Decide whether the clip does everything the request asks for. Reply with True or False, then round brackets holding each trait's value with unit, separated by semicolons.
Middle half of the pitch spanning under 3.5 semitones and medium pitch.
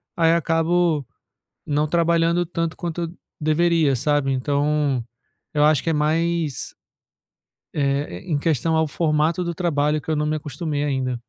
True (2.4 semitones; 155 Hz)